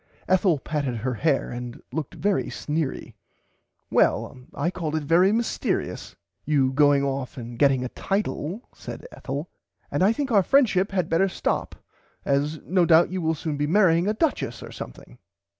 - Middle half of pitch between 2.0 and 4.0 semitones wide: No, average, 5.2 semitones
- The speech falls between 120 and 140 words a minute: No, average, 165 wpm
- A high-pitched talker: No, medium, 160 Hz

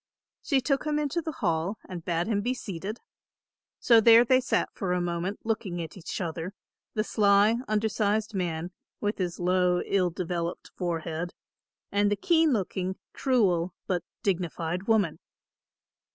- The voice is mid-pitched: No, high, 195 Hz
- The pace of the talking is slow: No, average, 150 wpm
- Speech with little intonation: No, average, 4.1 semitones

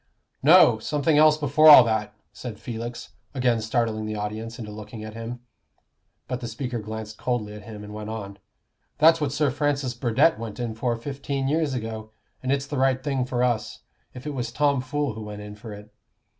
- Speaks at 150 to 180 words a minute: No, average, 195 wpm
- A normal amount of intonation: Yes, average, 4.0 semitones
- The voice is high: No, low, 120 Hz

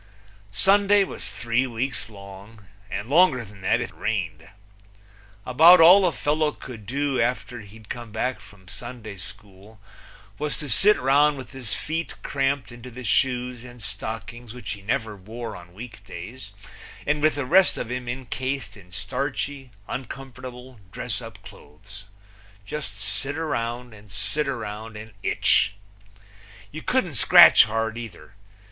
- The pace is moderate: Yes, average, 150 wpm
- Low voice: Yes, low, 120 Hz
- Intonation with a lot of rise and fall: No, average, 4.3 semitones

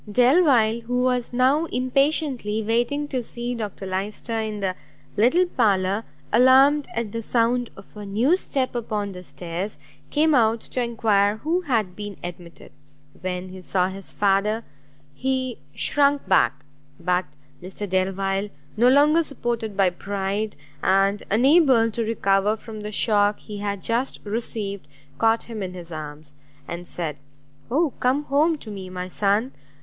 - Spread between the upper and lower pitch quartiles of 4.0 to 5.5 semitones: Yes, average, 4.4 semitones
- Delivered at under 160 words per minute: Yes, average, 150 wpm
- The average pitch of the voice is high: Yes, high, 220 Hz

